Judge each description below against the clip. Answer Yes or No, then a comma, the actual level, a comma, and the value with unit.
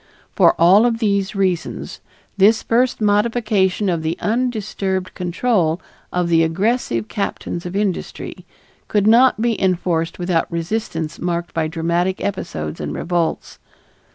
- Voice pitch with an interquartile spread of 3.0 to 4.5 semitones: Yes, average, 4.1 semitones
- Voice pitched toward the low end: No, medium, 185 Hz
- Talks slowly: Yes, slow, 125 wpm